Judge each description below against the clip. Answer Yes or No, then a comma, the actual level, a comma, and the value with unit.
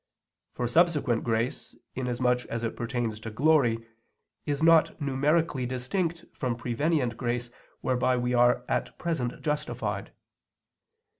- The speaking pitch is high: No, low, 125 Hz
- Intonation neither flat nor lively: Yes, average, 3.8 semitones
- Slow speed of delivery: Yes, slow, 120 wpm